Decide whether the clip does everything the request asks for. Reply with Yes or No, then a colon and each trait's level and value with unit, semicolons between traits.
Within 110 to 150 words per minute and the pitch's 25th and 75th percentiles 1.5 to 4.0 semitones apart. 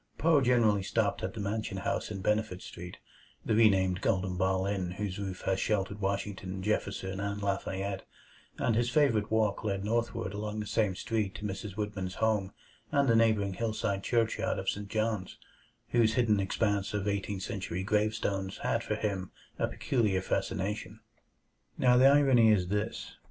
No: average, 160 wpm; narrow, 2.5 semitones